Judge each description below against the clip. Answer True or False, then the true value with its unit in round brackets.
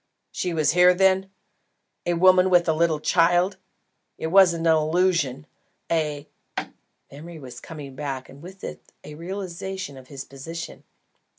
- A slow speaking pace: False (150 wpm)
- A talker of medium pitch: True (165 Hz)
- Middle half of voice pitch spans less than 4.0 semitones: True (3.5 semitones)